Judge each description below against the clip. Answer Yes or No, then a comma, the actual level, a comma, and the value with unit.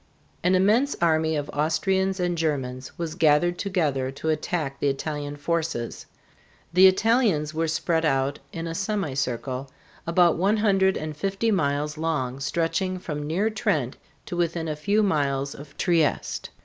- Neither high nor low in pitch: Yes, medium, 160 Hz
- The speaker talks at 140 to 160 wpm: Yes, average, 150 wpm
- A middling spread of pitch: Yes, average, 4.3 semitones